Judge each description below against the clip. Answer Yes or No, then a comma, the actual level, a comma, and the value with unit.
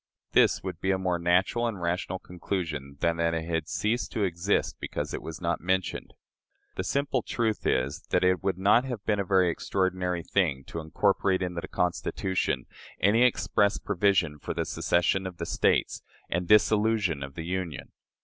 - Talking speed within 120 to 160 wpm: No, average, 175 wpm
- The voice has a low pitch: Yes, very low, 90 Hz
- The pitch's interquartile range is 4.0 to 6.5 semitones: No, average, 2.8 semitones